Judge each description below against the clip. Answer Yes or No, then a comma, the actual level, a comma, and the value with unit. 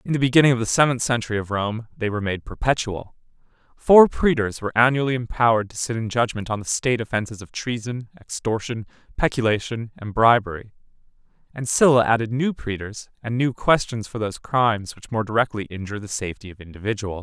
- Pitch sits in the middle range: No, low, 115 Hz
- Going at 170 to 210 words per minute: Yes, average, 180 wpm